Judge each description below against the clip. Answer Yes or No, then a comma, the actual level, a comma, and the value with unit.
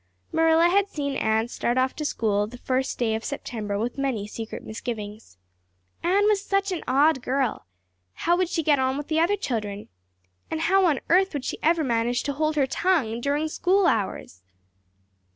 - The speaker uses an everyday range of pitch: No, wide, 6.3 semitones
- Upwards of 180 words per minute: Yes, average, 190 wpm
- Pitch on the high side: Yes, very high, 275 Hz